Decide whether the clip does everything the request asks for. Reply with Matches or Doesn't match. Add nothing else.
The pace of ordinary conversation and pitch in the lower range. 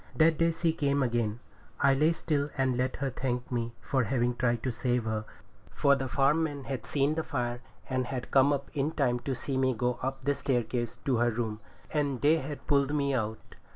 Doesn't match